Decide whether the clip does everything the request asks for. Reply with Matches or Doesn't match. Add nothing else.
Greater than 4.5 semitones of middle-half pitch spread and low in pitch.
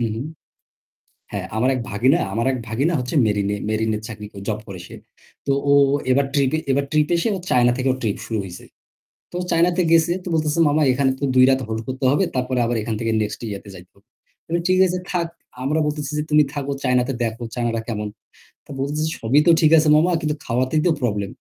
Matches